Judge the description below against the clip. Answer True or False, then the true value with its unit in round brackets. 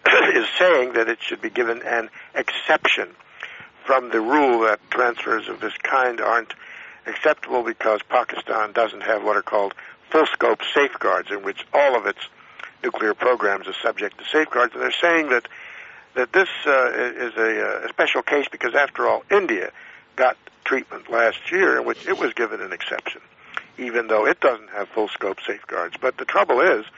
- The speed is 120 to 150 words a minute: False (170 wpm)